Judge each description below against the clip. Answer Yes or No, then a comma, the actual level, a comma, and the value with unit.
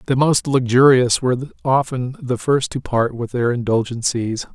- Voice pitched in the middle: No, low, 125 Hz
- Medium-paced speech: Yes, average, 160 wpm